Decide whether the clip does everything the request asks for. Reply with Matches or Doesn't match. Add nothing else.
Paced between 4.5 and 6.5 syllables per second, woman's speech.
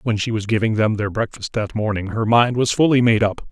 Doesn't match